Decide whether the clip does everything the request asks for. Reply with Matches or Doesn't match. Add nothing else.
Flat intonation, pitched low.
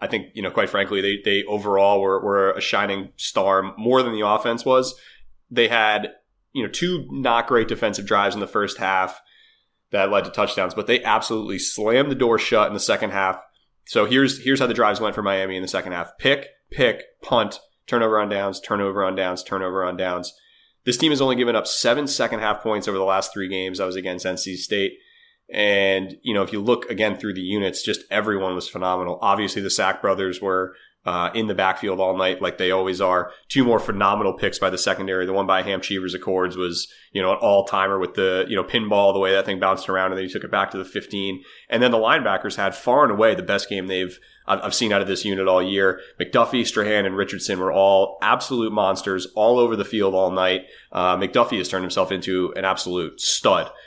Matches